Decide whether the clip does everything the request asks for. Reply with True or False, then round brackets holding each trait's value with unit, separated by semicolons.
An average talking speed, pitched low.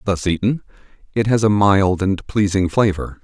True (165 wpm; 100 Hz)